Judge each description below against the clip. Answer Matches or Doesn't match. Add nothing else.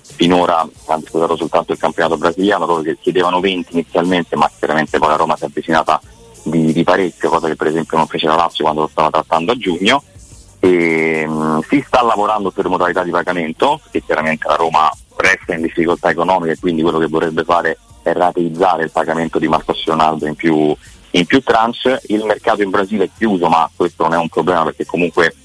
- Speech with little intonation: Matches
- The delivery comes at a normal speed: Doesn't match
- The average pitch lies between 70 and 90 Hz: Matches